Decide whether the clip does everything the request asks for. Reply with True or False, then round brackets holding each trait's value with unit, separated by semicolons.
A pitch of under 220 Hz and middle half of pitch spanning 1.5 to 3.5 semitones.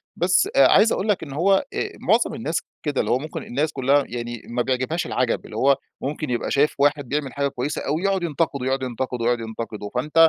False (140 Hz; 4.1 semitones)